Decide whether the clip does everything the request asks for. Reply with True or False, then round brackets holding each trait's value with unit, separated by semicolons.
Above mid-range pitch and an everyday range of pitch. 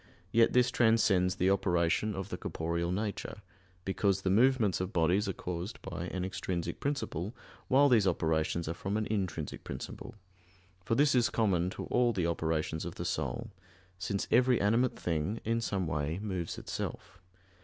False (95 Hz; 4.8 semitones)